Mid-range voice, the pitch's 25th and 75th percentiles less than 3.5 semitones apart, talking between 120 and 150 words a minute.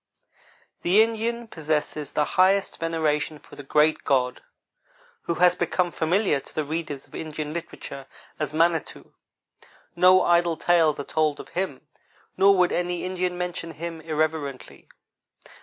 Yes: medium, 165 Hz; average, 2.8 semitones; average, 140 wpm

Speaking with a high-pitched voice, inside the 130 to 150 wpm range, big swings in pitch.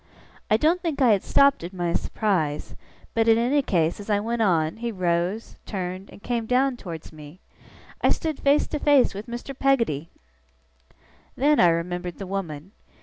No: high, 205 Hz; average, 175 wpm; wide, 6.2 semitones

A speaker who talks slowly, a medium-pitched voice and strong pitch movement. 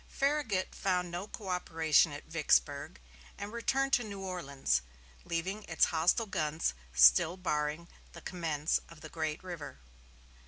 No: slow, 130 wpm; medium, 170 Hz; average, 4.0 semitones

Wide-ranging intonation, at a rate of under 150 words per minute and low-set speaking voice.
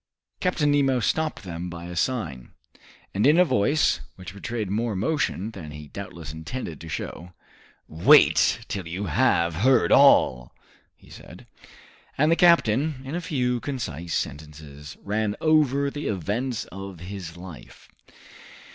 Yes: wide, 7.9 semitones; average, 140 wpm; low, 100 Hz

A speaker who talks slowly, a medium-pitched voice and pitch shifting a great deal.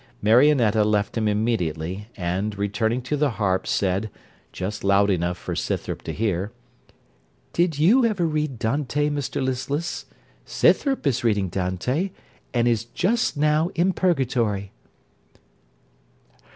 No: slow, 125 wpm; low, 115 Hz; wide, 6.7 semitones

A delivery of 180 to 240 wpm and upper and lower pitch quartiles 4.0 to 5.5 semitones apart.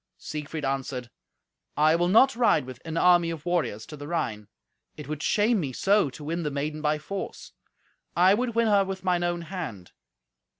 Yes: average, 185 wpm; average, 4.5 semitones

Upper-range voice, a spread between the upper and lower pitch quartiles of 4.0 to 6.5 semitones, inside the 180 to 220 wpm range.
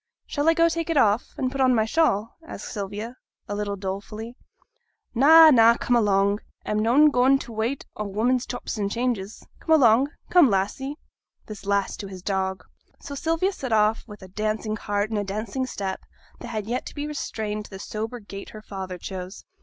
Yes: high, 220 Hz; average, 4.4 semitones; average, 195 wpm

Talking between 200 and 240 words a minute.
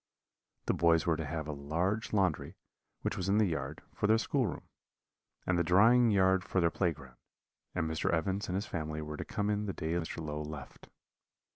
Yes: fast, 205 wpm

